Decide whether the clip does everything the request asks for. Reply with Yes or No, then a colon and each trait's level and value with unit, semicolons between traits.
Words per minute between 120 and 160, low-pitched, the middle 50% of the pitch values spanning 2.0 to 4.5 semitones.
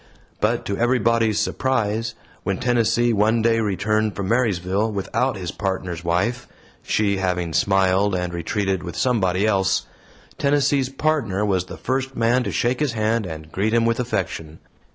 Yes: average, 155 wpm; low, 105 Hz; average, 3.7 semitones